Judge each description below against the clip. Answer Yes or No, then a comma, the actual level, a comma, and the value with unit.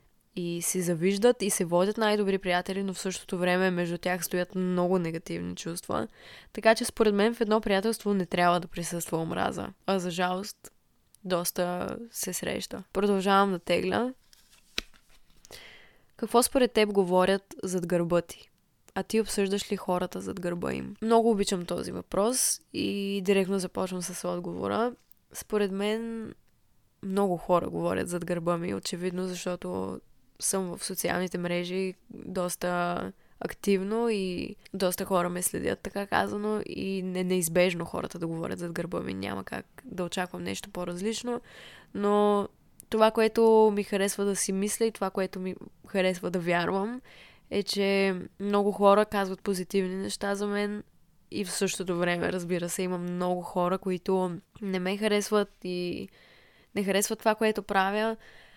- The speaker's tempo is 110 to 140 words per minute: No, average, 150 wpm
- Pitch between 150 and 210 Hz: Yes, high, 190 Hz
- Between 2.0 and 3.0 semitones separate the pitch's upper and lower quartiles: Yes, narrow, 2.4 semitones